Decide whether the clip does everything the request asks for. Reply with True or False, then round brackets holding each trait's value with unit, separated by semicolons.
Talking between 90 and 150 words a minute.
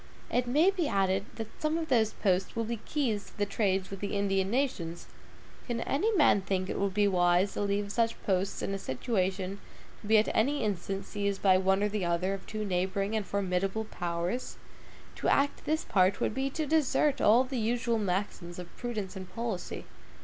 False (200 wpm)